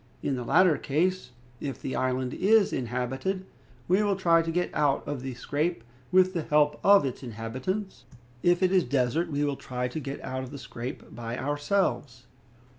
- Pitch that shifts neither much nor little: No, wide, 5.8 semitones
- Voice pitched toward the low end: No, medium, 145 Hz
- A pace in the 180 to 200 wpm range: Yes, average, 185 wpm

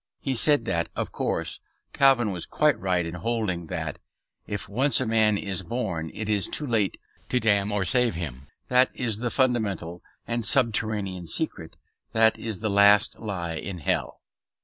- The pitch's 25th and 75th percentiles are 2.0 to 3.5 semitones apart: No, average, 4.4 semitones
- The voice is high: No, low, 105 Hz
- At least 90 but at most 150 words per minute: No, average, 170 wpm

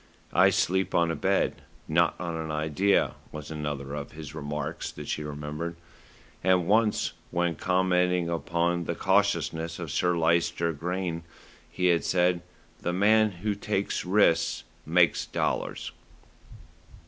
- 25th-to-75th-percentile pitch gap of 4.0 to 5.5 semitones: No, narrow, 2.5 semitones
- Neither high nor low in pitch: No, very low, 85 Hz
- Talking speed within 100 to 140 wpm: Yes, slow, 135 wpm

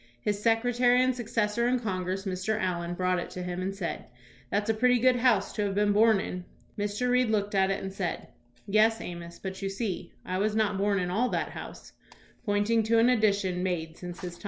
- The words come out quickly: Yes, fast, 220 wpm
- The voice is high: Yes, high, 205 Hz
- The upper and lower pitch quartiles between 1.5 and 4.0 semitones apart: Yes, average, 3.4 semitones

